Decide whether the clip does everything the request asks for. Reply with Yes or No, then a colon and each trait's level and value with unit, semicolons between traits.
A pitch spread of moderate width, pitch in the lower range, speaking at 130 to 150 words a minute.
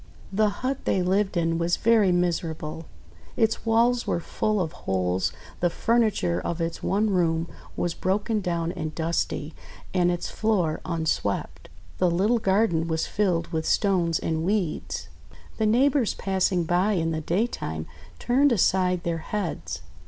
No: average, 4.2 semitones; medium, 175 Hz; average, 145 wpm